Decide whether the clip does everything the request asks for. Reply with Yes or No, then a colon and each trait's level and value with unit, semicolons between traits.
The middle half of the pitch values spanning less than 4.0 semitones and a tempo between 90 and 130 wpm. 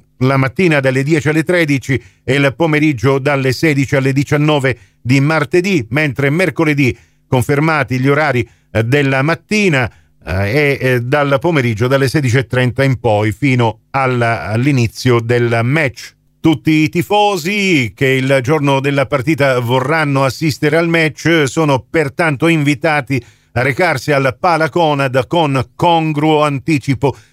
Yes: average, 3.4 semitones; average, 120 wpm